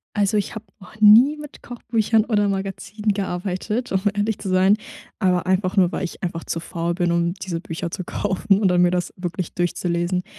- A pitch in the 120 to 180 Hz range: No, high, 190 Hz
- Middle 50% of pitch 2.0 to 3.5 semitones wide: Yes, average, 2.9 semitones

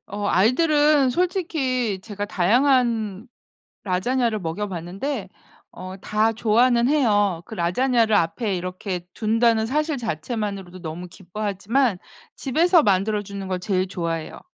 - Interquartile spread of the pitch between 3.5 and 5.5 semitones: Yes, average, 5.2 semitones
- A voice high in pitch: Yes, high, 215 Hz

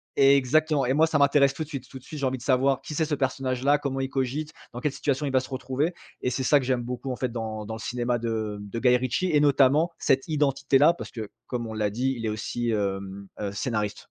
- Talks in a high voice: No, low, 130 Hz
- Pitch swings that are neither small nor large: Yes, average, 3.2 semitones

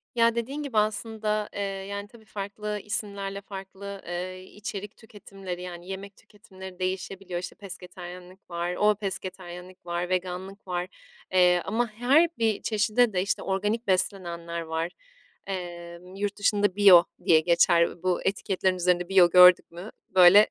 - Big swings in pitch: No, narrow, 2.5 semitones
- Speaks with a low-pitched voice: No, high, 190 Hz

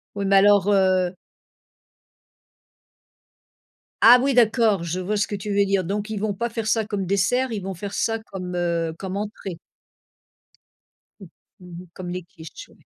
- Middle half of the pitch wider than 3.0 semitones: No, narrow, 2.6 semitones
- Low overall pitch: No, high, 195 Hz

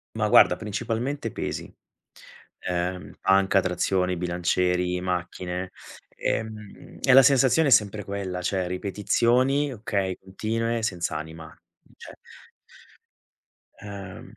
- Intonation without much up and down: No, average, 3.9 semitones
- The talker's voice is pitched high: No, very low, 95 Hz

